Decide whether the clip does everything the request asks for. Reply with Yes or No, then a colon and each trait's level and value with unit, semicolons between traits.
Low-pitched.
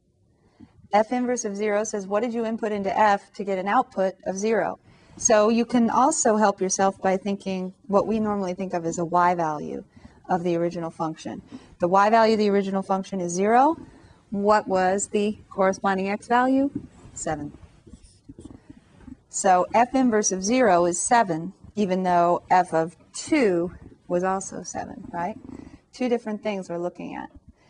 No: high, 200 Hz